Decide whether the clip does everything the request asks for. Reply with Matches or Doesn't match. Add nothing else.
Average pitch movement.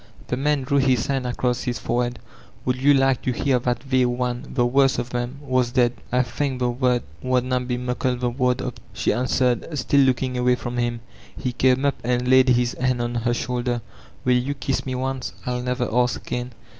Doesn't match